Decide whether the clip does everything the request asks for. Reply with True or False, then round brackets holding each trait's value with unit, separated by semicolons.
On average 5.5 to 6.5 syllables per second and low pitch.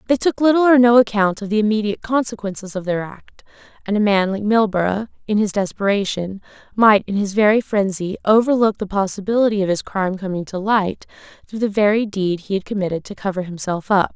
False (5.8 syllables/s; 205 Hz)